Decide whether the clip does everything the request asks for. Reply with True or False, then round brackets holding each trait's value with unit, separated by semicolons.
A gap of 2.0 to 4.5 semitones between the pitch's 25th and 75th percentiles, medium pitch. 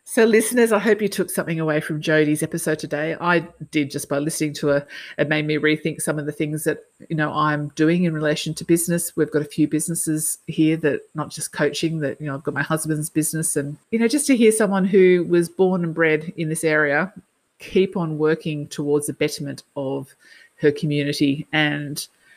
True (2.4 semitones; 155 Hz)